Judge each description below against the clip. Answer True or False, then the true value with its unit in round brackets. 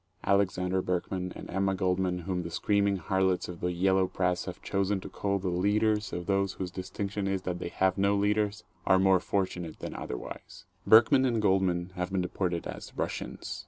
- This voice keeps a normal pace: True (185 wpm)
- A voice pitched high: False (95 Hz)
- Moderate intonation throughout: False (1.7 semitones)